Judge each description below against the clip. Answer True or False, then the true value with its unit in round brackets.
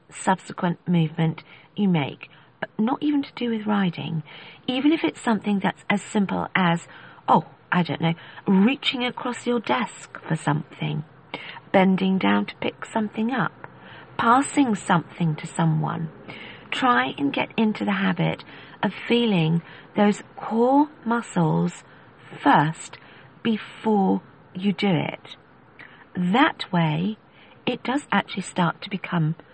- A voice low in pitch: False (180 Hz)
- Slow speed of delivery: True (130 wpm)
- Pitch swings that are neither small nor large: False (5.8 semitones)